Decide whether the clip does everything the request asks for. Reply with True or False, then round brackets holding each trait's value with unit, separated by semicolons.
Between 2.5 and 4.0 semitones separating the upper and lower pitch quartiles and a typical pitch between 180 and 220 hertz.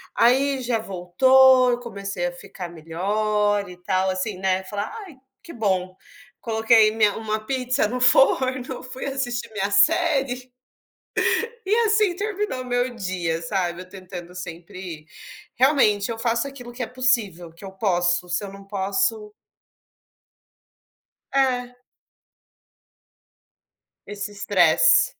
False (5.2 semitones; 215 Hz)